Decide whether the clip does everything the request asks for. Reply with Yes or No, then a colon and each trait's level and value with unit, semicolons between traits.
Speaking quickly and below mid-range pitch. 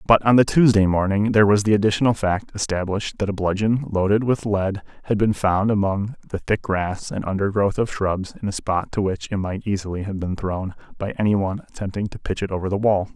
Yes: fast, 225 wpm; low, 100 Hz